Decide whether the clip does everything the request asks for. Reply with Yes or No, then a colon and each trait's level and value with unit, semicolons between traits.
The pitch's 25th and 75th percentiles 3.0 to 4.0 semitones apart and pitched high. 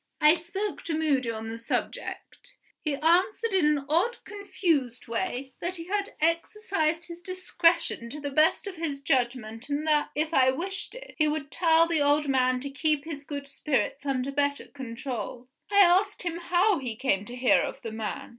No: average, 4.6 semitones; very high, 300 Hz